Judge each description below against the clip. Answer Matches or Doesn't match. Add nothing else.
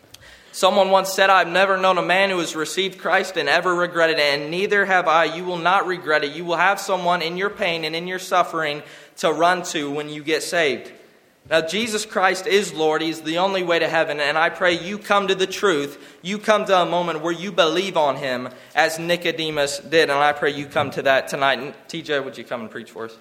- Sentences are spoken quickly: Matches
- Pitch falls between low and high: Matches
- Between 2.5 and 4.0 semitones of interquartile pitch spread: Matches